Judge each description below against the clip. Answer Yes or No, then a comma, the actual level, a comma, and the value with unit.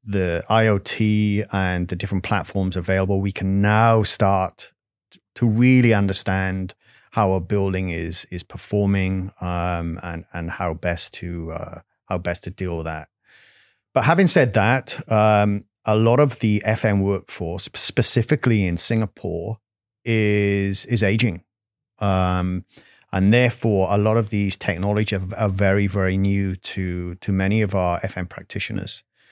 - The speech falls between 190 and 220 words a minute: No, average, 140 wpm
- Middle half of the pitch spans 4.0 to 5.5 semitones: No, average, 3.0 semitones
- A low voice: Yes, low, 100 Hz